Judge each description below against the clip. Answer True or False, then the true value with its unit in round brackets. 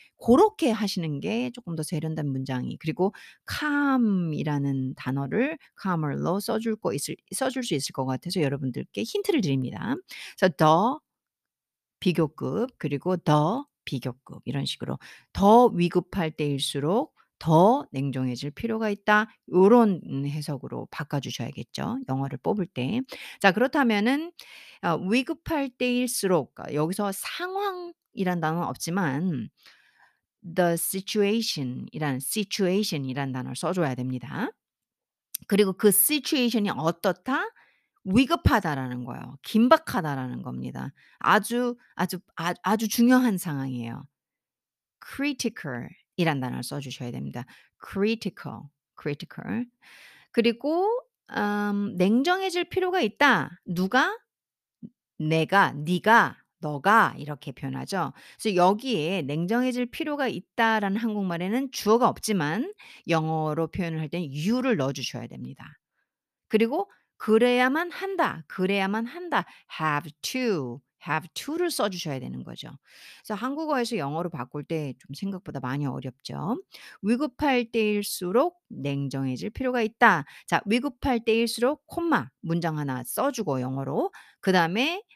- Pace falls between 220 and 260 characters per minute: False (305 characters per minute)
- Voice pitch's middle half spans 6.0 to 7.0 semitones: False (8.4 semitones)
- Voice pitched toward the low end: False (190 Hz)